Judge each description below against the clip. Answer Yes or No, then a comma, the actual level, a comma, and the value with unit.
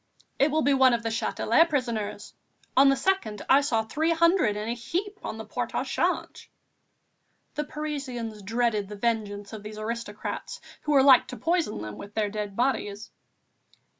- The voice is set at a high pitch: Yes, high, 235 Hz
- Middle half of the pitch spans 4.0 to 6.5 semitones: Yes, average, 5.2 semitones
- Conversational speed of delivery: Yes, average, 175 wpm